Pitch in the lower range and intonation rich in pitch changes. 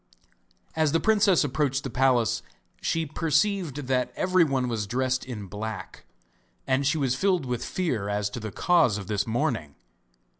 Yes: low, 130 Hz; wide, 6.2 semitones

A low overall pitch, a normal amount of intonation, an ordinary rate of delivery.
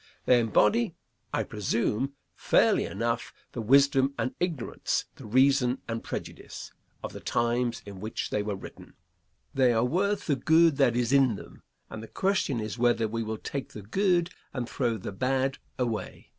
Yes: low, 125 Hz; average, 3.6 semitones; average, 170 wpm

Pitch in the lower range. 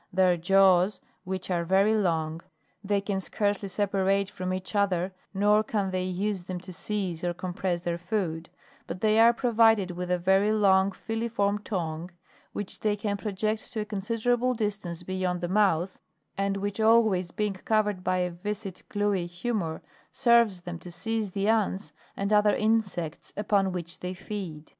No: high, 195 Hz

